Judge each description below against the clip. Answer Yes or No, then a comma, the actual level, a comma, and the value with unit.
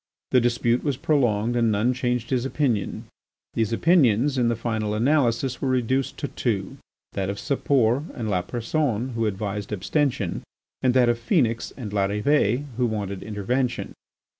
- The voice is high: No, low, 120 Hz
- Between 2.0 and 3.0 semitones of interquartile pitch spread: No, average, 3.6 semitones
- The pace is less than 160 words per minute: Yes, average, 150 wpm